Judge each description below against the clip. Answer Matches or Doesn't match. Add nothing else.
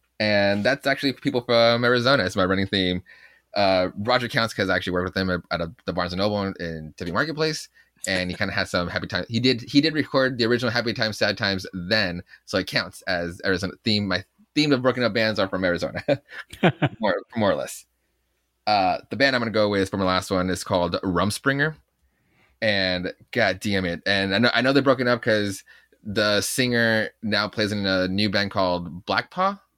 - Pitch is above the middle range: Doesn't match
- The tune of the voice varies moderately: Matches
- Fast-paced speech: Matches